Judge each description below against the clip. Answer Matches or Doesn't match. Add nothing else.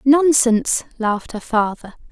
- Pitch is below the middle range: Doesn't match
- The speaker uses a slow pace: Matches